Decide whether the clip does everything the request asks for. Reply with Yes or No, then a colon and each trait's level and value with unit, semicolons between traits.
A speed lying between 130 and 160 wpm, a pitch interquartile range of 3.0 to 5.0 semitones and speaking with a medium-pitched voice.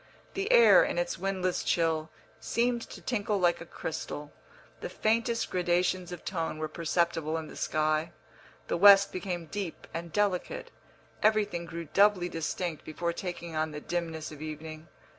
Yes: average, 155 wpm; average, 3.7 semitones; medium, 175 Hz